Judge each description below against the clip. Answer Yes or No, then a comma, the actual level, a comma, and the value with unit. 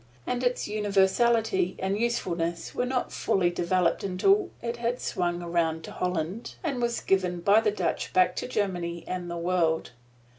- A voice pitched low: No, high, 190 Hz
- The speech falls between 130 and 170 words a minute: Yes, average, 160 wpm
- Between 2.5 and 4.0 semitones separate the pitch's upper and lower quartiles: No, average, 5.1 semitones